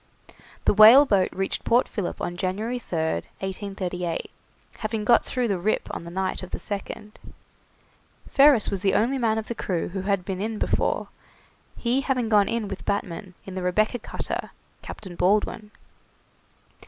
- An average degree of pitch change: Yes, average, 3.3 semitones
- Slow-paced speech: No, average, 160 wpm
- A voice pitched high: Yes, high, 205 Hz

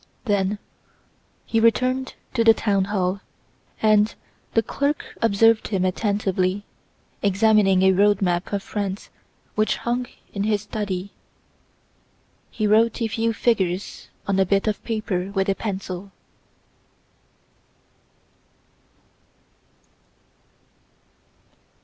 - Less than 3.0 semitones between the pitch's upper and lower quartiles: Yes, narrow, 2.5 semitones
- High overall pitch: Yes, high, 205 Hz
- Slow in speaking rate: Yes, slow, 100 wpm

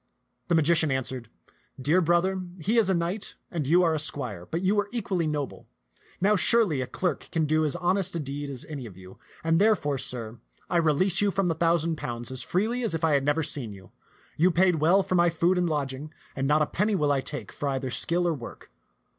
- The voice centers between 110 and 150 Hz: No, medium, 160 Hz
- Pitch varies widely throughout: No, average, 4.4 semitones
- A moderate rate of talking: No, fast, 230 wpm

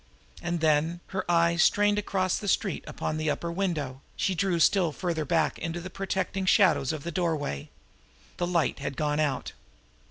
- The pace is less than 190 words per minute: Yes, average, 170 wpm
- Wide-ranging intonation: No, average, 3.2 semitones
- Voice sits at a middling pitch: Yes, medium, 170 Hz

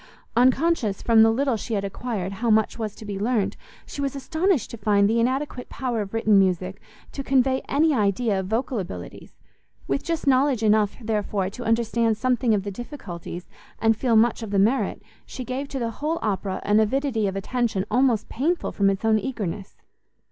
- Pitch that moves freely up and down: No, average, 4.2 semitones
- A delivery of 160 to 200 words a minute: Yes, average, 190 wpm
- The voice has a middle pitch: No, high, 225 Hz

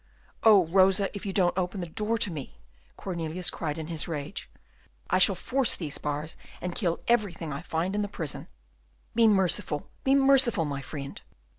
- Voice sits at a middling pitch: Yes, medium, 180 Hz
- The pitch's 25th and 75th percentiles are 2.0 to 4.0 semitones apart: No, average, 4.5 semitones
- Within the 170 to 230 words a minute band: Yes, average, 175 wpm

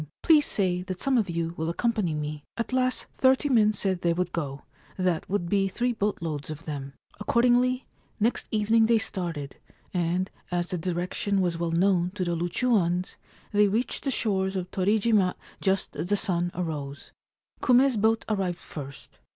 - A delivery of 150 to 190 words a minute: Yes, average, 170 wpm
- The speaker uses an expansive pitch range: No, average, 4.4 semitones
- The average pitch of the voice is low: No, medium, 185 Hz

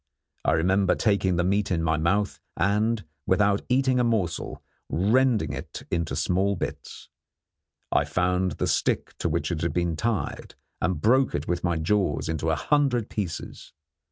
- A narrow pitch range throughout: No, average, 4.1 semitones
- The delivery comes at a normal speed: Yes, average, 160 wpm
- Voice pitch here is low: Yes, very low, 95 Hz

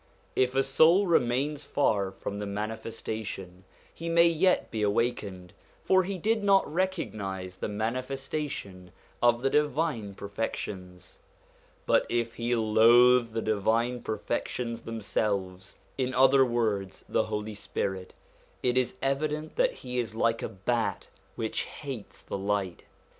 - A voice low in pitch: Yes, low, 115 Hz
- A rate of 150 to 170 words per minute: No, slow, 135 wpm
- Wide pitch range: No, average, 4.8 semitones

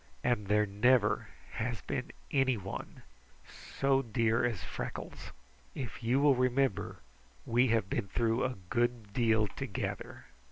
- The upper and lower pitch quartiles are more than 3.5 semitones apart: No, average, 3.1 semitones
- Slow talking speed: Yes, slow, 125 wpm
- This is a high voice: No, low, 115 Hz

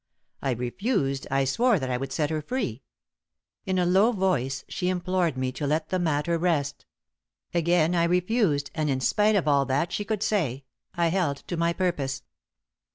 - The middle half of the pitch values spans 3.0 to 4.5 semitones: No, average, 5.1 semitones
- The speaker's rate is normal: Yes, average, 180 wpm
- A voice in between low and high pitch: Yes, medium, 165 Hz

